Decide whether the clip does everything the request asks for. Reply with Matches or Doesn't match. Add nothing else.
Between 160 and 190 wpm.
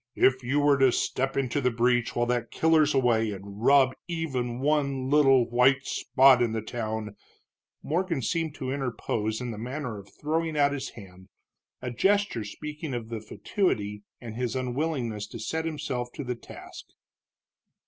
Matches